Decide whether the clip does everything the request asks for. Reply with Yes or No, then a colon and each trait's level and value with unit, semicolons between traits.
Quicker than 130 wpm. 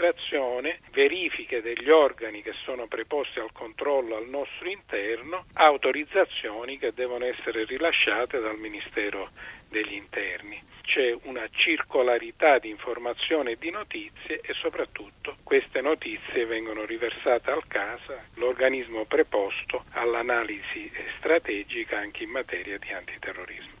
No: slow, 115 wpm